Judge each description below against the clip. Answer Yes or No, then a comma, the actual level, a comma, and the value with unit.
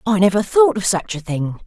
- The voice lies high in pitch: Yes, high, 200 Hz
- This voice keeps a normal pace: No, fast, 255 wpm